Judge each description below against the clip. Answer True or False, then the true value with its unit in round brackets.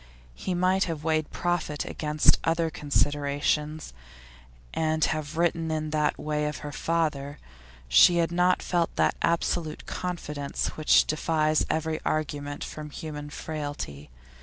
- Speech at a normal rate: False (130 wpm)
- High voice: False (155 Hz)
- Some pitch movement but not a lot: False (1.9 semitones)